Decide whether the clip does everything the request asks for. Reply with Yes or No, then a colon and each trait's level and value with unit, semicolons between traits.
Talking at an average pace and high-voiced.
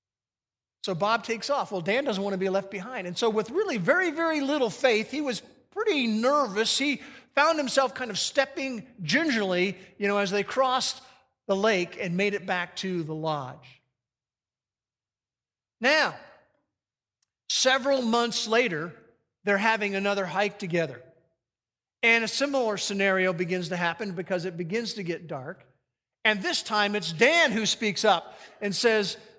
Yes: average, 155 wpm; high, 205 Hz